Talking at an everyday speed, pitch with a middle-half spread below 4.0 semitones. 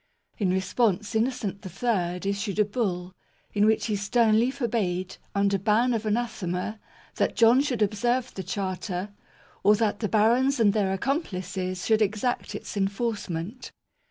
Yes: average, 150 wpm; average, 3.4 semitones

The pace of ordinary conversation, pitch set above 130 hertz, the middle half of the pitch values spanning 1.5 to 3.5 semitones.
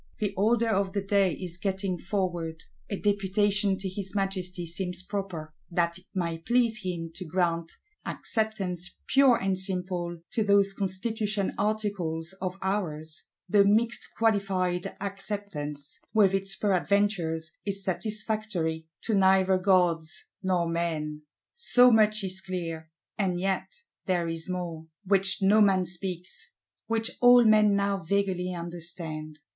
No: slow, 130 wpm; high, 190 Hz; average, 2.8 semitones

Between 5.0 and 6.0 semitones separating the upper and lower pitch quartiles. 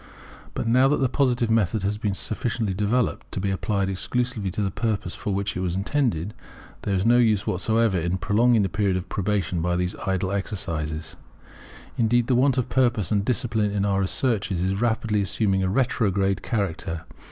No: average, 3.5 semitones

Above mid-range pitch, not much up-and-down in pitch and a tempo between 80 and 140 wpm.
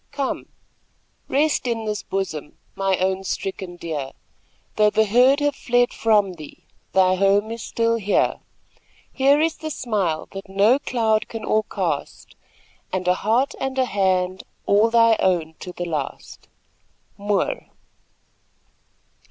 No: high, 210 Hz; average, 4.0 semitones; slow, 135 wpm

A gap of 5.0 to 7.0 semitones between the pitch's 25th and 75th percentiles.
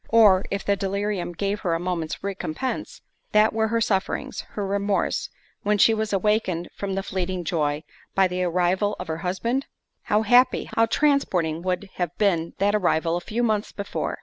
No: average, 3.0 semitones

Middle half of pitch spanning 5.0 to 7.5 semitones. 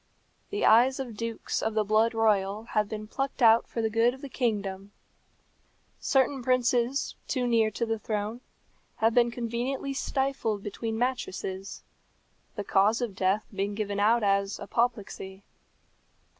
No: average, 2.9 semitones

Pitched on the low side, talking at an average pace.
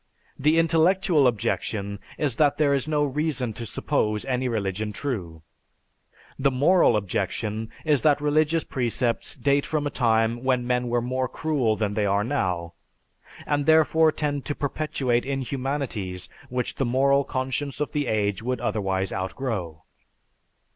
Yes: low, 130 Hz; average, 145 wpm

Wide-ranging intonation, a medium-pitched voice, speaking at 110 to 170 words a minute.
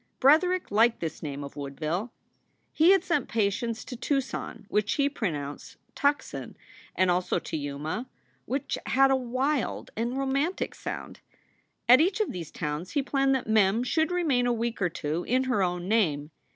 No: wide, 7.5 semitones; high, 235 Hz; average, 165 wpm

